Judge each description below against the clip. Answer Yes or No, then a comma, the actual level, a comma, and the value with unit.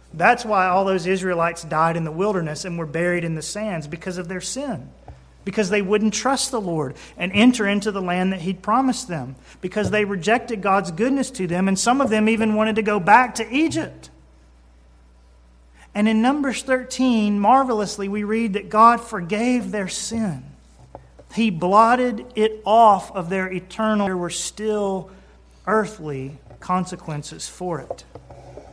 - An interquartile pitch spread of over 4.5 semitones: No, average, 4.0 semitones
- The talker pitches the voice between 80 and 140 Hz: No, high, 200 Hz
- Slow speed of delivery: No, average, 165 wpm